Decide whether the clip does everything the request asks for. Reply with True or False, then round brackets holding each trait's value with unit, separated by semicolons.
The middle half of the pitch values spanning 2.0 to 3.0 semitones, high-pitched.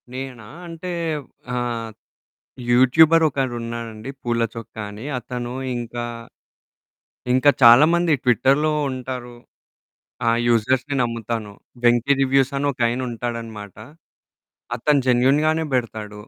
False (2.7 semitones; 120 Hz)